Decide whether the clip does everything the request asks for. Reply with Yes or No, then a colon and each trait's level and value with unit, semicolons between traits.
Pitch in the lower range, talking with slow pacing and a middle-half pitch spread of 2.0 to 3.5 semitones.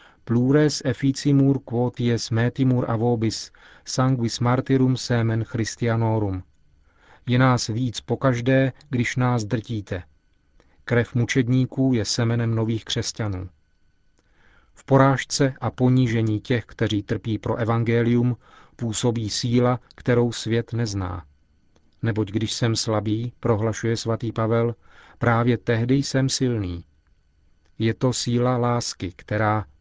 Yes: low, 115 Hz; slow, 105 wpm; narrow, 2.6 semitones